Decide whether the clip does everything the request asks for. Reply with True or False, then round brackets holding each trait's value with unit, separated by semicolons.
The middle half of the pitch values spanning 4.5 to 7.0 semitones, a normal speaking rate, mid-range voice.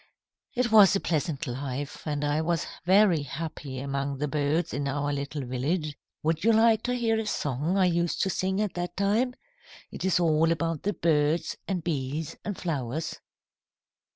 True (4.8 semitones; 175 wpm; 160 Hz)